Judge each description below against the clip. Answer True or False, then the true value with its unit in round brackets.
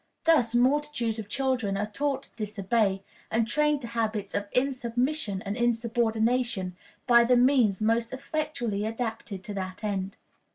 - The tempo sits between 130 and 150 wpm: True (140 wpm)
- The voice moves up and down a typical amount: True (3.4 semitones)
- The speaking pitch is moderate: False (230 Hz)